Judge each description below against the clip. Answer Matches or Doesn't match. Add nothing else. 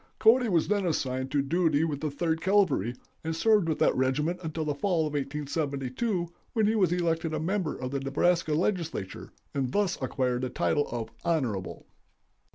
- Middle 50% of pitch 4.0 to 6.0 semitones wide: Matches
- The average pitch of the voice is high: Doesn't match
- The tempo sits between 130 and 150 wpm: Doesn't match